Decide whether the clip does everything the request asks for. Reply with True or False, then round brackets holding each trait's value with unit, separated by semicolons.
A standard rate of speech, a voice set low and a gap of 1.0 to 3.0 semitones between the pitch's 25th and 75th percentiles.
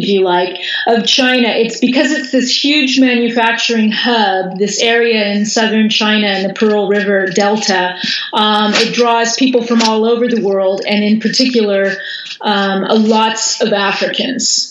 False (155 wpm; 220 Hz; 2.4 semitones)